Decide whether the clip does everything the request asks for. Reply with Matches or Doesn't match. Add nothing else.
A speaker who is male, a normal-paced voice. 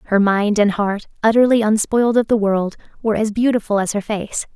Doesn't match